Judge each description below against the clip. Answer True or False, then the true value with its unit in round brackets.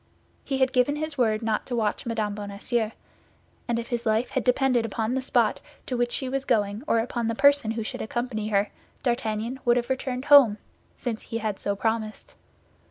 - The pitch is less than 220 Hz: False (235 Hz)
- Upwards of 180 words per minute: True (195 wpm)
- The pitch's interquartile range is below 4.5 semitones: True (2.7 semitones)